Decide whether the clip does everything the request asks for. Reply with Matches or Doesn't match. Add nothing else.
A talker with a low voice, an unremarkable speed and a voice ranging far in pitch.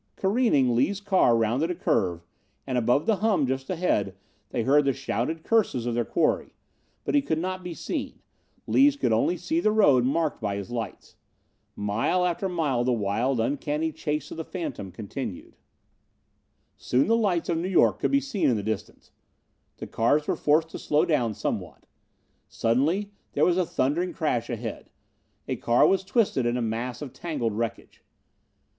Doesn't match